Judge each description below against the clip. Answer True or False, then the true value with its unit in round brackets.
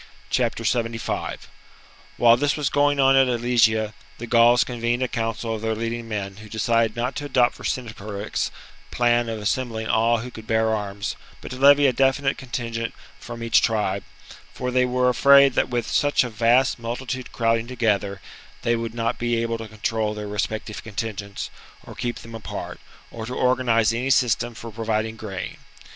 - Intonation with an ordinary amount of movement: False (2.1 semitones)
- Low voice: True (115 Hz)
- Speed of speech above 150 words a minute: True (170 wpm)